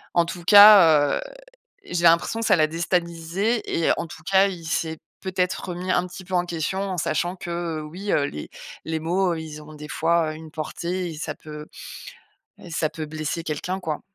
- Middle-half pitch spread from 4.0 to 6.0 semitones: No, narrow, 2.5 semitones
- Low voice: No, medium, 170 Hz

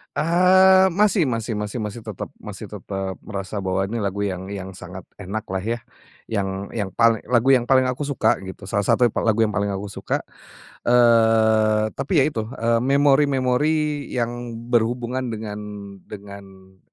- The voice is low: Yes, low, 115 Hz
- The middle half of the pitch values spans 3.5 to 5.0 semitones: Yes, average, 4.3 semitones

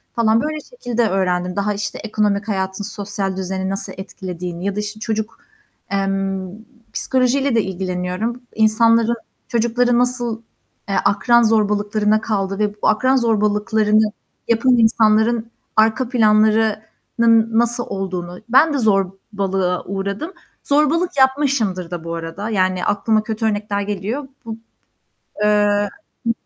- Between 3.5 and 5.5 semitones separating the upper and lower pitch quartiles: No, average, 3.0 semitones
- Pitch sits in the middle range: No, high, 215 Hz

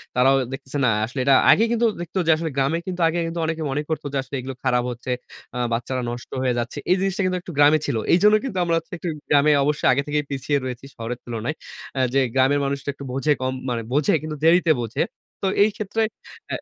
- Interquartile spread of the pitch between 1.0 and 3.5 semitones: No, average, 4.2 semitones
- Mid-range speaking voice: Yes, medium, 145 Hz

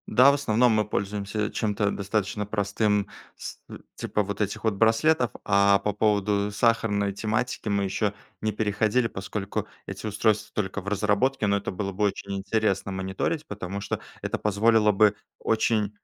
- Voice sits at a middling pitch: No, low, 105 Hz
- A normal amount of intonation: No, narrow, 1.5 semitones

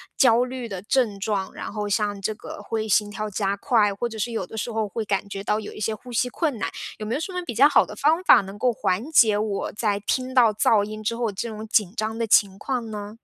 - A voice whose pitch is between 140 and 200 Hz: No, high, 215 Hz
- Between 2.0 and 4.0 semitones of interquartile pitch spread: Yes, narrow, 2.5 semitones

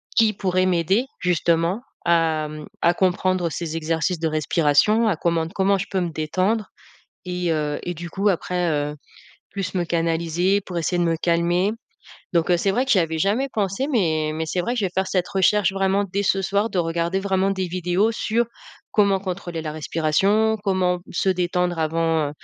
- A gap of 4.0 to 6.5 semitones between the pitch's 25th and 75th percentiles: No, average, 2.9 semitones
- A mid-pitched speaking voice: Yes, medium, 180 Hz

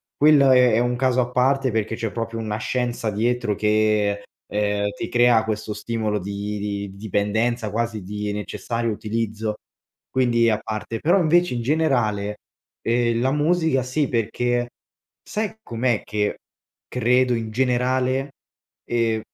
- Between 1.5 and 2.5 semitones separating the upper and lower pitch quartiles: No, average, 2.9 semitones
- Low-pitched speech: Yes, low, 115 Hz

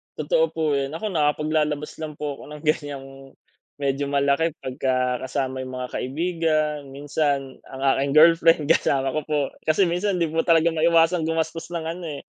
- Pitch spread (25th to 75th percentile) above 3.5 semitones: No, average, 2.9 semitones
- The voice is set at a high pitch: No, medium, 150 Hz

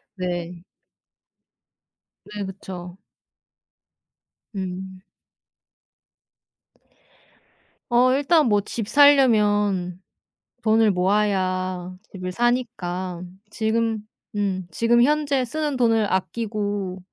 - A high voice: Yes, high, 205 Hz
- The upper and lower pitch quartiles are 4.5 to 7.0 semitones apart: No, average, 4.1 semitones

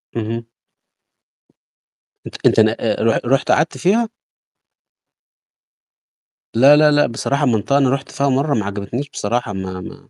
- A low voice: Yes, low, 130 Hz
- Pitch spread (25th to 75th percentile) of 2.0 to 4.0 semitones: No, average, 4.5 semitones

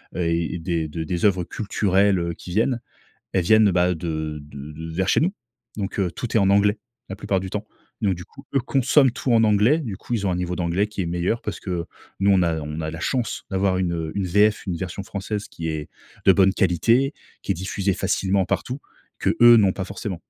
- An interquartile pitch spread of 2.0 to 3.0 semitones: No, average, 3.5 semitones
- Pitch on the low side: Yes, very low, 95 Hz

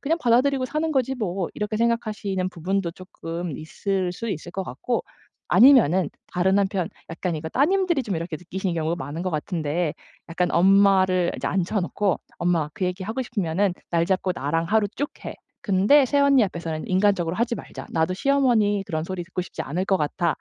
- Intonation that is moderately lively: Yes, average, 4.3 semitones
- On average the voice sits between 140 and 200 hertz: Yes, high, 190 Hz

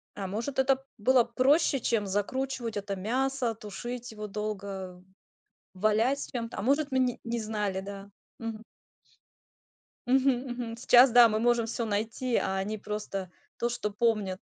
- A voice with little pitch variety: No, average, 3.4 semitones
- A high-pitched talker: Yes, high, 230 Hz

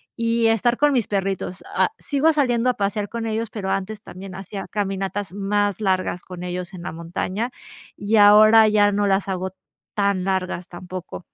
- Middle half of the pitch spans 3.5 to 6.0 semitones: No, average, 2.7 semitones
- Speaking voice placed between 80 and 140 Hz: No, high, 200 Hz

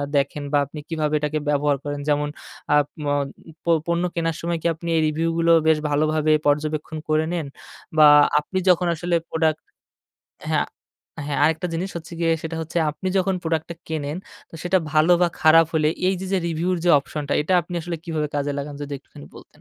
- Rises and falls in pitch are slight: Yes, narrow, 2.3 semitones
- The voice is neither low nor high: Yes, medium, 155 Hz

